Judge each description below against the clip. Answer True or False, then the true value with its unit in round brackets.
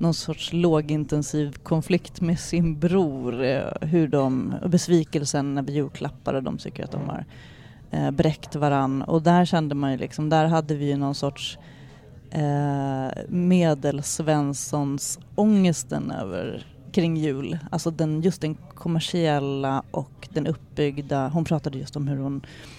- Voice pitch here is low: False (150 Hz)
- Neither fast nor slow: True (135 wpm)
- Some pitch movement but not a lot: True (3.0 semitones)